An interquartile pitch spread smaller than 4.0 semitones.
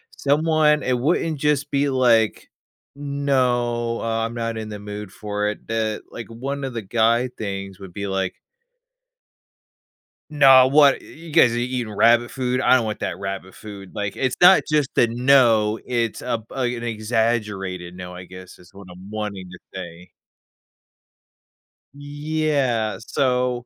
No: average, 4.4 semitones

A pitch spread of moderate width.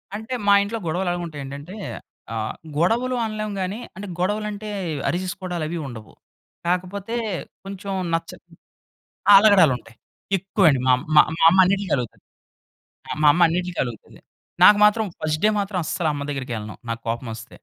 No: wide, 5.7 semitones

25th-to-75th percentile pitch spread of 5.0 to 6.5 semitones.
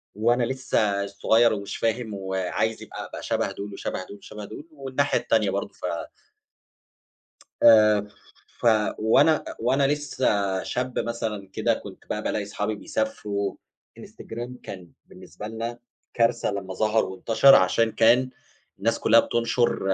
No: average, 3.0 semitones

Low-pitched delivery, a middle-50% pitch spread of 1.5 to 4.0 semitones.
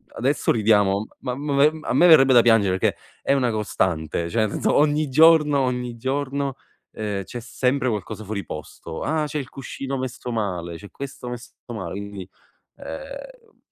No: low, 125 Hz; wide, 5.4 semitones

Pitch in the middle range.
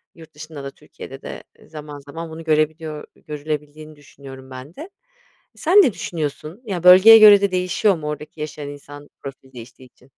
Yes: medium, 155 Hz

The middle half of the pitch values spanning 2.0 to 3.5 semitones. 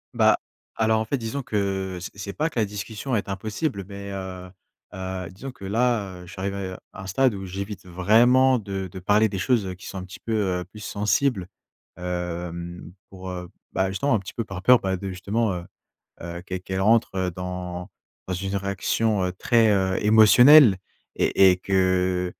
Yes: average, 2.9 semitones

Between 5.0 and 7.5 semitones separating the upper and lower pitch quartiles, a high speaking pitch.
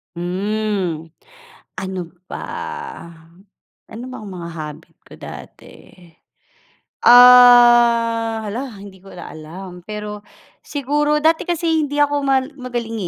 Yes: wide, 5.6 semitones; high, 225 Hz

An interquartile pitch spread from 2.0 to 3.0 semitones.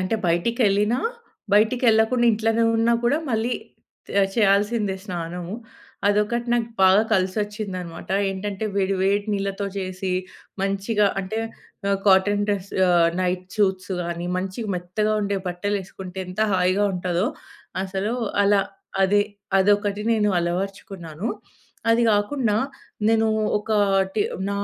Yes: narrow, 2.4 semitones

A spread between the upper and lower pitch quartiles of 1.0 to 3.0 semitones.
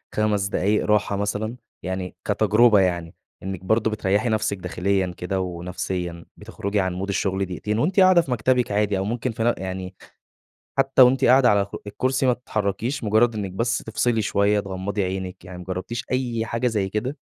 No: average, 3.6 semitones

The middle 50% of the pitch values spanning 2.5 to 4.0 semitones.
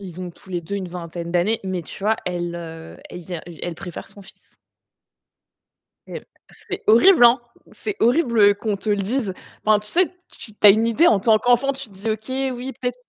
No: average, 5.1 semitones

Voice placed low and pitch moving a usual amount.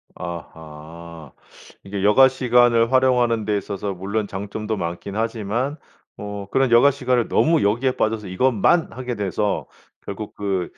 Yes: low, 105 Hz; average, 4.0 semitones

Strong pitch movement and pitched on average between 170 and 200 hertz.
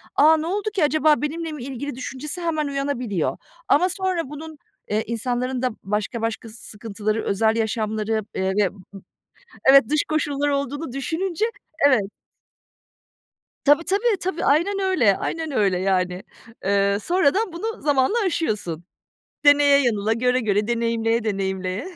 No: wide, 6.4 semitones; very high, 260 Hz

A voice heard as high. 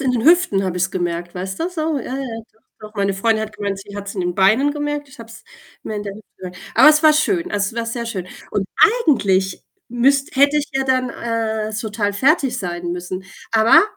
Yes: high, 220 Hz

